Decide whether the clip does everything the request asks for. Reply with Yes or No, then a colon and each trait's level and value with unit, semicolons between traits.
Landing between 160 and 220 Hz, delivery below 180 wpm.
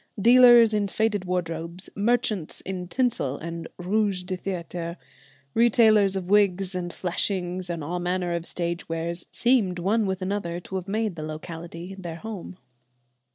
Yes: medium, 185 Hz; average, 150 wpm